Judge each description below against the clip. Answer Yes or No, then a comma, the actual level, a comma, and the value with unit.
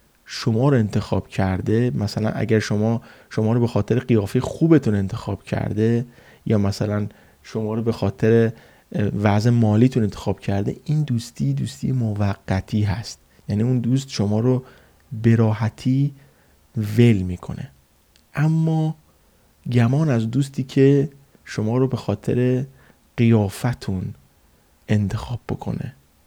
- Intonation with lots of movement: No, average, 3.5 semitones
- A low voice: Yes, low, 110 Hz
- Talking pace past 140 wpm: No, average, 115 wpm